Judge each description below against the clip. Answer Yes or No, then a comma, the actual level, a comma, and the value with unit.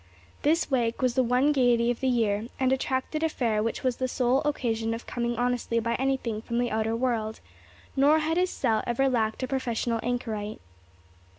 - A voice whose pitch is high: Yes, high, 245 Hz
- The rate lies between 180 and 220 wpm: Yes, average, 190 wpm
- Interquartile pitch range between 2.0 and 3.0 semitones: Yes, narrow, 2.5 semitones